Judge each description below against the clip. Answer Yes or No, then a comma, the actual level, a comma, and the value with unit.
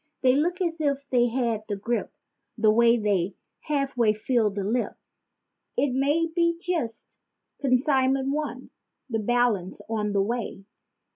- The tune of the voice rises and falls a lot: No, average, 4.5 semitones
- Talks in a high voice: Yes, high, 245 Hz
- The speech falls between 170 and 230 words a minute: No, average, 145 wpm